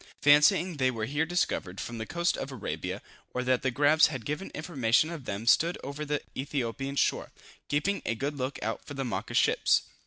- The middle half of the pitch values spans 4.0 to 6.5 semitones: No, average, 3.4 semitones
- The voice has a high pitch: No, medium, 140 Hz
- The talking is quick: Yes, fast, 210 wpm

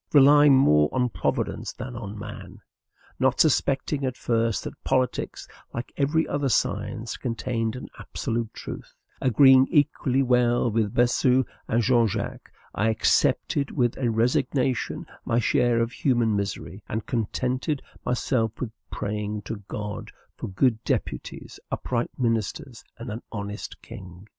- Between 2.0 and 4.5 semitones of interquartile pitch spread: Yes, average, 2.9 semitones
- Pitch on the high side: No, low, 120 Hz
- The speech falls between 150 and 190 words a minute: No, slow, 135 wpm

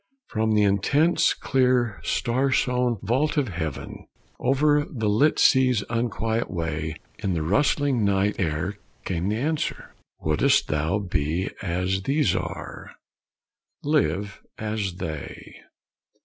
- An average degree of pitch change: No, wide, 6.0 semitones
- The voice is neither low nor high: No, low, 105 Hz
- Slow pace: Yes, slow, 120 wpm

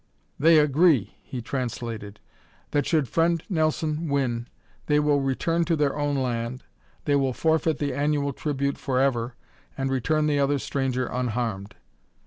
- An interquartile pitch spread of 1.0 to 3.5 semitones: Yes, average, 3.2 semitones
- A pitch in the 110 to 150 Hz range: Yes, medium, 140 Hz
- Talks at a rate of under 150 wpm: Yes, average, 140 wpm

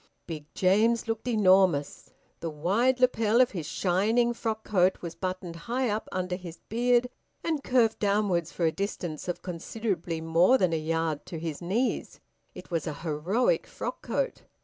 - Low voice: No, medium, 185 Hz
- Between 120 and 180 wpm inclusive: Yes, average, 165 wpm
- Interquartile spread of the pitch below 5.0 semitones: No, wide, 5.4 semitones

